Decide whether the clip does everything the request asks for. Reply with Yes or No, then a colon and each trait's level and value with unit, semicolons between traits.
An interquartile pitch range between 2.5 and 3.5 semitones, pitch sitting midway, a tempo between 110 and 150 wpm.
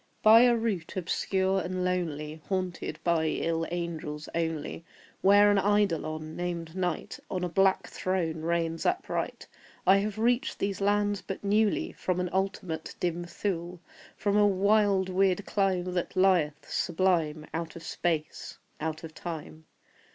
Yes: average, 3.1 semitones; medium, 180 Hz; average, 145 wpm